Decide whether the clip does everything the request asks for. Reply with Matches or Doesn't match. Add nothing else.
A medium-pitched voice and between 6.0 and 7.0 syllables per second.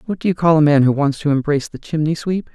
Matches